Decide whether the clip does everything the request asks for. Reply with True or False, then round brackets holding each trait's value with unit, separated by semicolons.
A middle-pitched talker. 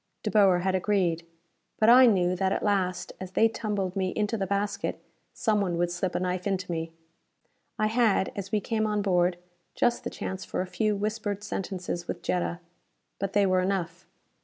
False (195 Hz)